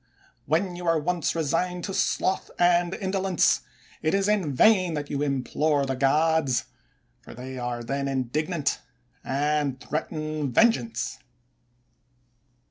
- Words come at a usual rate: No, slow, 125 wpm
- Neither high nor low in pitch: Yes, medium, 155 Hz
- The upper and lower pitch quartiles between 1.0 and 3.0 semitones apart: No, average, 4.5 semitones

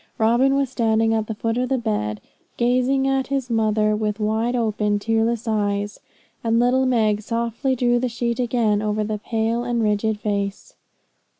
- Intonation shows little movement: Yes, narrow, 2.3 semitones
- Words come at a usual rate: Yes, average, 170 wpm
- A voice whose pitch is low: No, high, 225 Hz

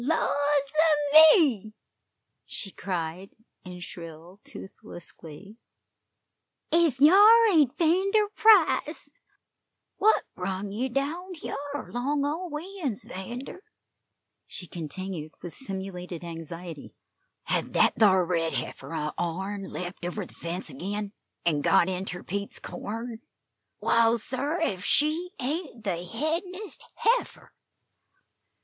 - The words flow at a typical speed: No, slow, 115 wpm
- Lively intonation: Yes, wide, 9.0 semitones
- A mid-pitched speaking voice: No, high, 215 Hz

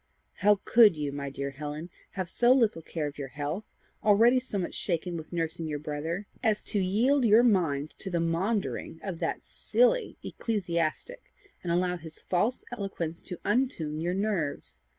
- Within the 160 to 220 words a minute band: Yes, average, 170 wpm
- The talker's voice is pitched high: No, medium, 180 Hz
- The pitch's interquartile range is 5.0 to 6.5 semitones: Yes, average, 5.3 semitones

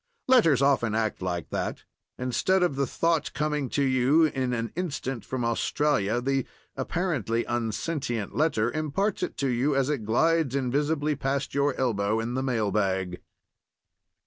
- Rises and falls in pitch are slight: No, average, 4.4 semitones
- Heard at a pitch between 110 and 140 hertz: Yes, low, 135 Hz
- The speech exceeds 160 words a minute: No, average, 150 wpm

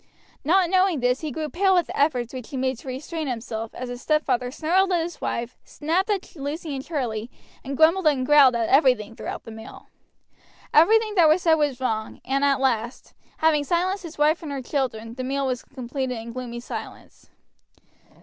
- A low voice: No, very high, 275 Hz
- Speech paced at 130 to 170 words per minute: No, average, 195 wpm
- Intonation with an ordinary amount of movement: Yes, average, 4.4 semitones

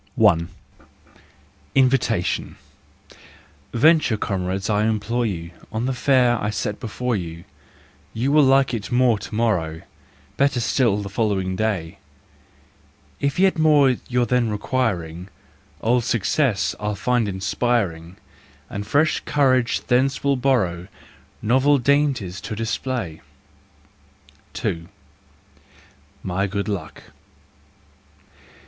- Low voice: Yes, low, 115 Hz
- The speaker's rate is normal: No, slow, 110 wpm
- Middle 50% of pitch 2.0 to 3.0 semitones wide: No, average, 4.8 semitones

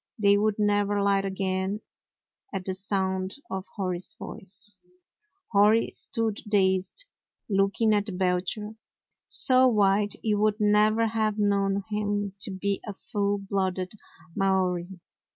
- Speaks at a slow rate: Yes, slow, 125 wpm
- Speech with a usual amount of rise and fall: No, narrow, 1.7 semitones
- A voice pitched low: No, high, 200 Hz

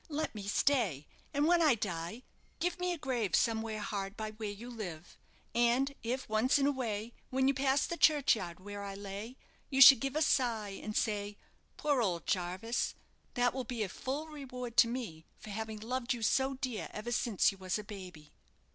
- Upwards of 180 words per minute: Yes, average, 195 wpm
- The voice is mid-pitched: No, high, 230 Hz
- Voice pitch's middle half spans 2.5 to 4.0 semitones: No, average, 4.6 semitones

